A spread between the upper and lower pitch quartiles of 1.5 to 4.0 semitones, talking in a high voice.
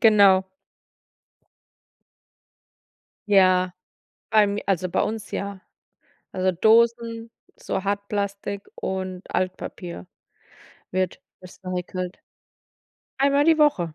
Yes: average, 3.0 semitones; high, 195 Hz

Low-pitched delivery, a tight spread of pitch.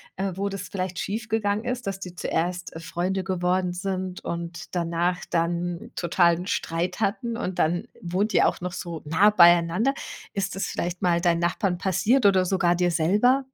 No: medium, 180 Hz; narrow, 2.3 semitones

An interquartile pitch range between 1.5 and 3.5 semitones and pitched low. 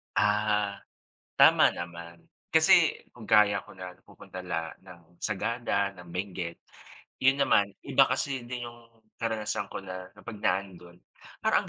Yes: average, 2.9 semitones; low, 100 Hz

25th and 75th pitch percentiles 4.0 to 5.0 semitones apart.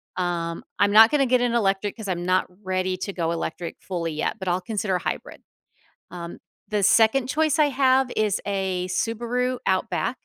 Yes: average, 4.7 semitones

